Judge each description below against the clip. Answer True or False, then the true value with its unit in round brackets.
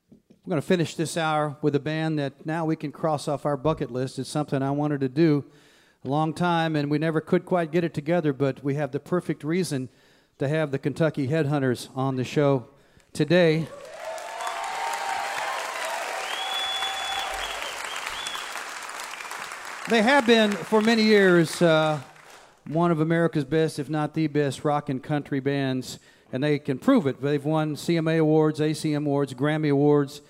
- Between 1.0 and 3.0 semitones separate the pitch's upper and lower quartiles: True (2.4 semitones)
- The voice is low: False (150 Hz)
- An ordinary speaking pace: True (160 wpm)